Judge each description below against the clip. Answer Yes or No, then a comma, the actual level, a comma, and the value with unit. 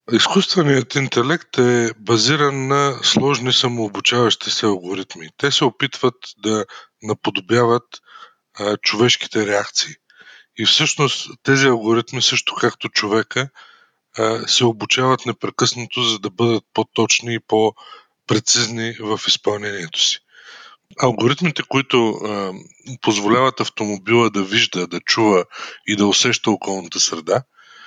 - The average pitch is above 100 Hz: Yes, low, 115 Hz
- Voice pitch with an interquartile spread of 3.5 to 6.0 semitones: No, average, 3.1 semitones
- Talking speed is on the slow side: Yes, slow, 110 wpm